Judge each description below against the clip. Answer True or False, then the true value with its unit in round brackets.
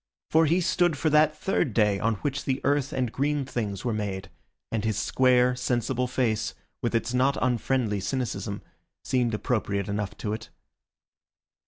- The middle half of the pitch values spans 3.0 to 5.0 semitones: True (4.0 semitones)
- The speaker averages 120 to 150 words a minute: False (160 wpm)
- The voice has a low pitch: True (125 Hz)